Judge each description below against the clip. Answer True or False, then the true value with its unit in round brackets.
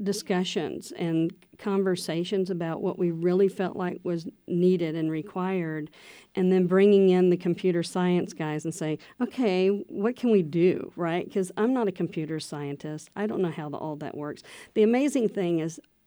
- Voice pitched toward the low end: False (180 Hz)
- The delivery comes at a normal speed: True (175 wpm)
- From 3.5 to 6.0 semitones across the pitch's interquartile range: False (3.1 semitones)